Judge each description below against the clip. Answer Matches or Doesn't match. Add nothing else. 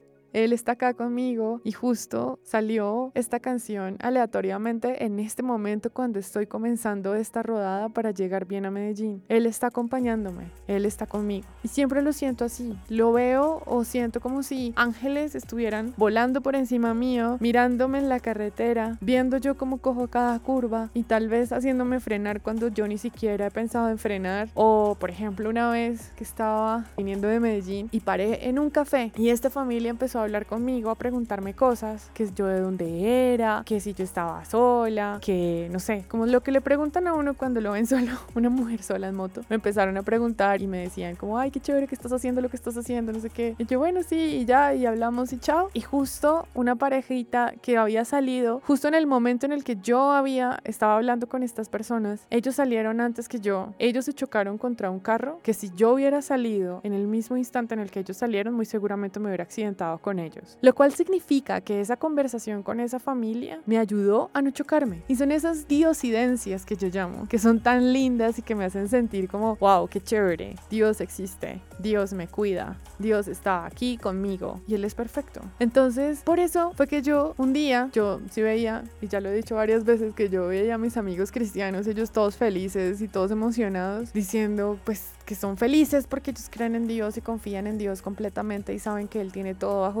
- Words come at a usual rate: Doesn't match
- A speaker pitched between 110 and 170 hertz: Doesn't match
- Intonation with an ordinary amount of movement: Matches